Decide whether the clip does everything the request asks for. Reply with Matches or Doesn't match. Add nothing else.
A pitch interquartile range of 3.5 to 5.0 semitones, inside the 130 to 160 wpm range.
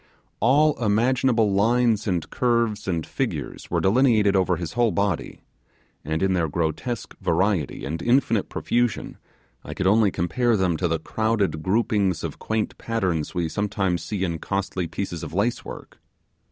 Matches